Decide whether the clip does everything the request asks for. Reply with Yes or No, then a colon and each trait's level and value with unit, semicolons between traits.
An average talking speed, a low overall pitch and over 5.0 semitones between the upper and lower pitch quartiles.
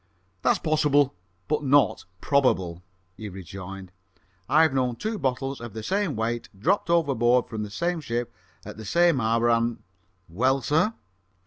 Yes: average, 150 wpm; low, 125 Hz; wide, 5.4 semitones